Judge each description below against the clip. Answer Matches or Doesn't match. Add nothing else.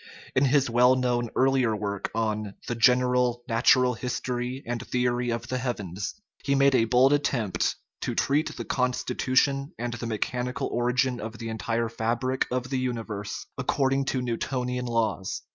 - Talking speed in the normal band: Matches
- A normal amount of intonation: Doesn't match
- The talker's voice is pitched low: Matches